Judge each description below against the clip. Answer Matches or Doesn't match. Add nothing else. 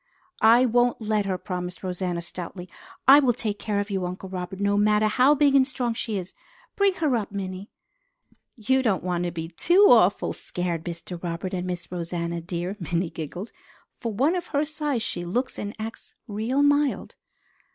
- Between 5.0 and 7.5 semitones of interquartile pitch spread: Matches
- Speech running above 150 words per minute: Matches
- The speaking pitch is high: Matches